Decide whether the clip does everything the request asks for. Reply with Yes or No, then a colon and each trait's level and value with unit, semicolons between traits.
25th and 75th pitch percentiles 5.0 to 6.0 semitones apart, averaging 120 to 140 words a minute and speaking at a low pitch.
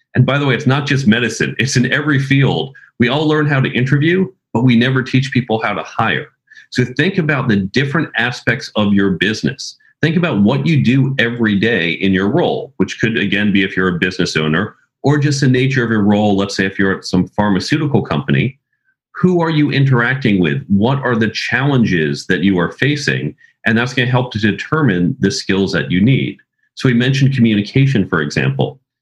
No: average, 5.3 semitones; fast, 205 wpm; low, 120 Hz